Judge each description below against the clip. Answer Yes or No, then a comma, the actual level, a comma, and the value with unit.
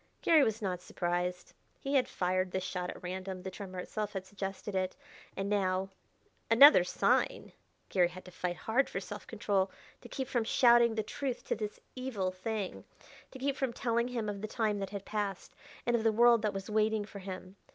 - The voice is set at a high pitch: Yes, high, 205 Hz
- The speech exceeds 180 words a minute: Yes, average, 200 wpm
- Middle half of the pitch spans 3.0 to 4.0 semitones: Yes, average, 3.6 semitones